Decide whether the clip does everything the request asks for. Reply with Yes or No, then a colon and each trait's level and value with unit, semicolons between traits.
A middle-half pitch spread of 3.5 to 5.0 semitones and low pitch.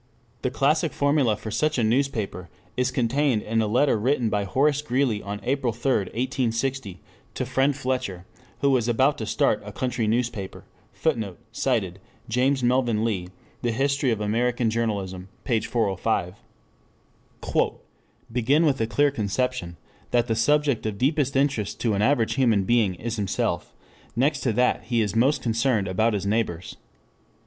Yes: average, 3.9 semitones; low, 120 Hz